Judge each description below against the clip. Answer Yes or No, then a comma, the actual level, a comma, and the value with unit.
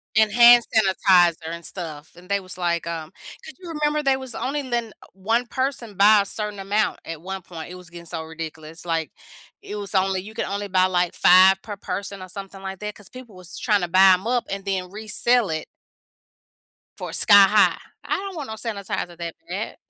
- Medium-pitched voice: No, high, 195 Hz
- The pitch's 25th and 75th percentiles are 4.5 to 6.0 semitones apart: No, average, 3.7 semitones